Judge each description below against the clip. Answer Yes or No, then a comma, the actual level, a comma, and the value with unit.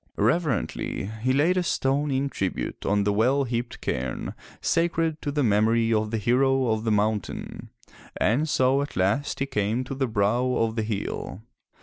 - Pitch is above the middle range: No, low, 120 Hz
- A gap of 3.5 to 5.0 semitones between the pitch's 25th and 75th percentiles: Yes, average, 4.4 semitones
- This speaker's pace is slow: No, average, 175 wpm